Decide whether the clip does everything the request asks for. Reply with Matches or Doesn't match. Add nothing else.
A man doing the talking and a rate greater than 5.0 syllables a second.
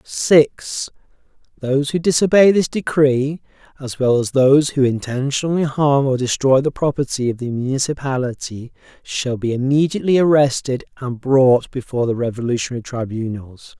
Matches